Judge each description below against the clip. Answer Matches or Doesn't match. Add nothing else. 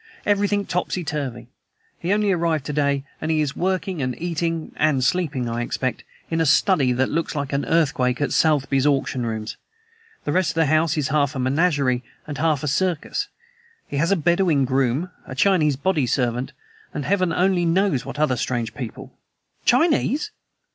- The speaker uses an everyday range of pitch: Matches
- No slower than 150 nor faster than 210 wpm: Matches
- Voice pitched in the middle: Matches